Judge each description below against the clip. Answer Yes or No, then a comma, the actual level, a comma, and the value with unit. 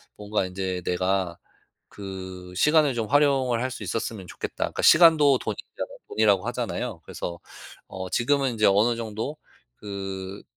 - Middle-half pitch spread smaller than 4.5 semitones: No, wide, 5.5 semitones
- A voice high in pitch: No, low, 105 Hz